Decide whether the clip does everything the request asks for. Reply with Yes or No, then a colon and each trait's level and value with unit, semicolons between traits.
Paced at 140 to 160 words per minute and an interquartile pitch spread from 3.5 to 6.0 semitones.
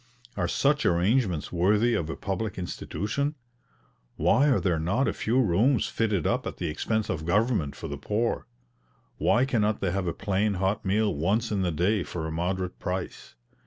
No: average, 180 wpm; average, 4.3 semitones